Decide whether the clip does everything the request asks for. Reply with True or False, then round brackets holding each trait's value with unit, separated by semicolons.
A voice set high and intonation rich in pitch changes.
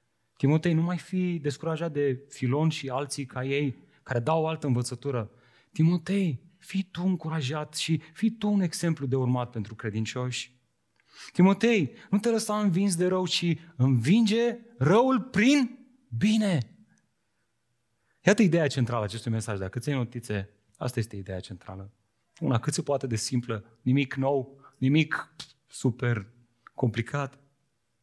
False (140 Hz; 6.4 semitones)